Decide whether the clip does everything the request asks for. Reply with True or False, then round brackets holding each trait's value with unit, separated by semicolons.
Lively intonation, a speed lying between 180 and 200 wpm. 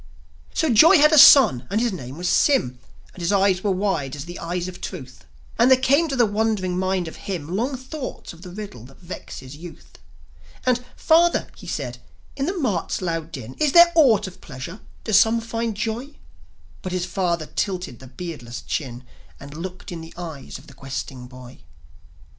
True (7.2 semitones; 190 wpm)